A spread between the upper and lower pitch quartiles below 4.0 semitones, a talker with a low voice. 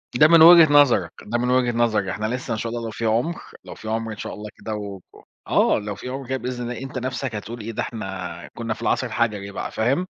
Yes: average, 3.0 semitones; low, 115 Hz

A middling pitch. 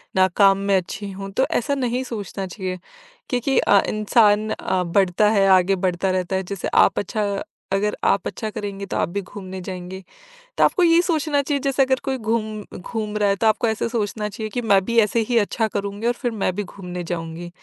No: high, 205 Hz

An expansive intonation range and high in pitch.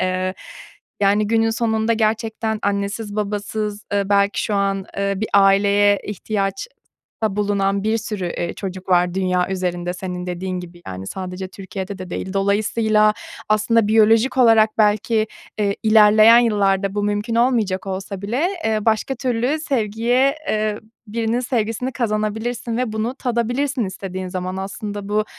No: narrow, 2.4 semitones; high, 210 Hz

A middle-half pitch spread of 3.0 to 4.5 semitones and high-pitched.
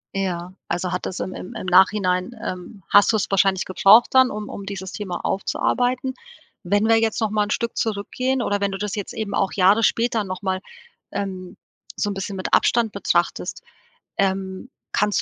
No: narrow, 2.6 semitones; high, 200 Hz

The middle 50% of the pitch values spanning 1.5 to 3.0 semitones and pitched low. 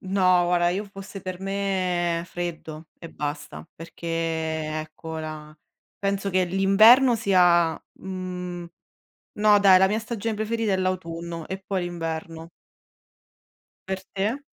No: average, 2.7 semitones; medium, 185 Hz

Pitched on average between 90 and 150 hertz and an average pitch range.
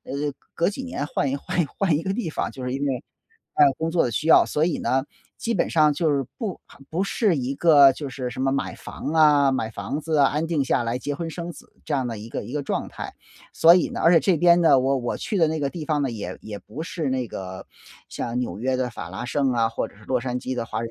Yes: medium, 140 Hz; average, 4.4 semitones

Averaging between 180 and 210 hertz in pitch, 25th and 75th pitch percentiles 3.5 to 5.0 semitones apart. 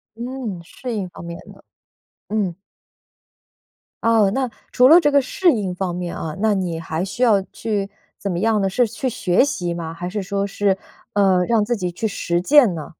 Yes: high, 200 Hz; average, 4.5 semitones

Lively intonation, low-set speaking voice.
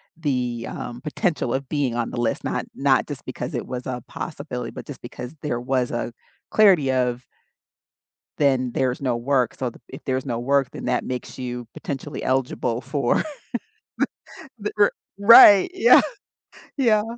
No: average, 2.8 semitones; low, 130 Hz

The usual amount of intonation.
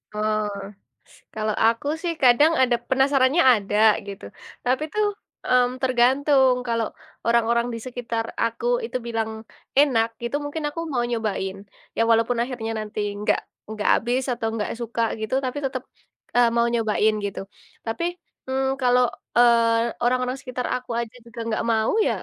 No: narrow, 2.3 semitones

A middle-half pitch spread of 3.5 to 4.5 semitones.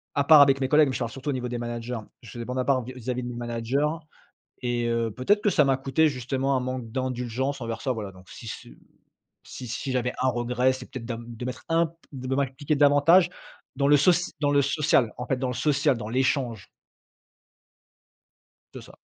No: average, 2.8 semitones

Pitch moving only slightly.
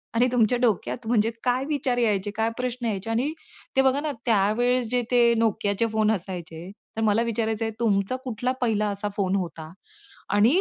No: average, 3.3 semitones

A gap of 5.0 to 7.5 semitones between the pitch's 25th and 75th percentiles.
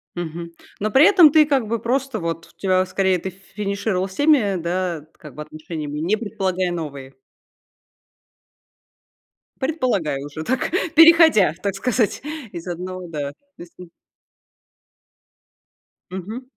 Yes: wide, 5.6 semitones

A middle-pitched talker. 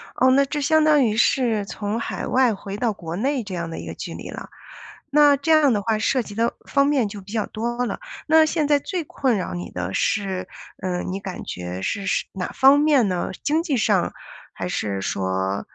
No: high, 220 Hz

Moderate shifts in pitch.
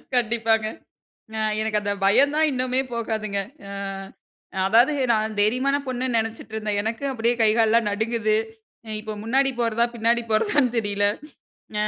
No: narrow, 2.3 semitones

